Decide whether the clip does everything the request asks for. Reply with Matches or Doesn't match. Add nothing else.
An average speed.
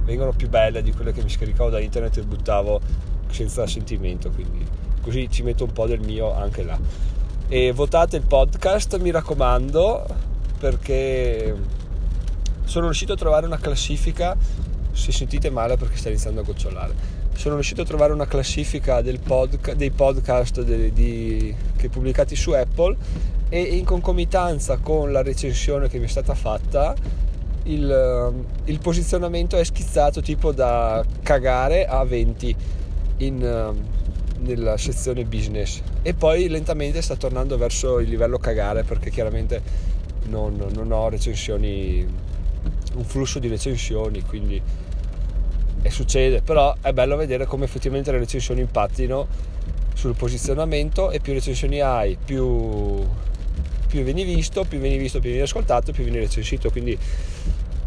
Matches